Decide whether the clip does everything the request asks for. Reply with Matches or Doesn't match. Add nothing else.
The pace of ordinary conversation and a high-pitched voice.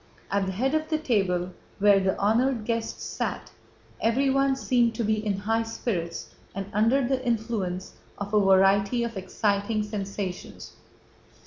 Matches